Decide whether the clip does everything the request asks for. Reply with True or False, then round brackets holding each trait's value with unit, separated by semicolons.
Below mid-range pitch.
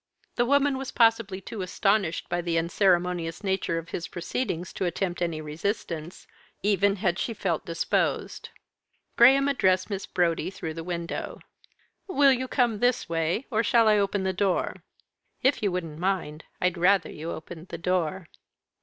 False (185 Hz)